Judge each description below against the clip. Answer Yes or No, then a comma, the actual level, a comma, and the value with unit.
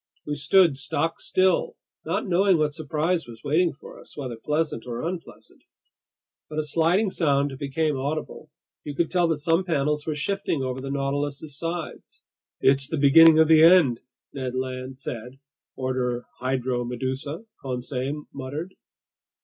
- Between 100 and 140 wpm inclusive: No, average, 150 wpm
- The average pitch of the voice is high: No, medium, 145 Hz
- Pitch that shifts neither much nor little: Yes, average, 3.7 semitones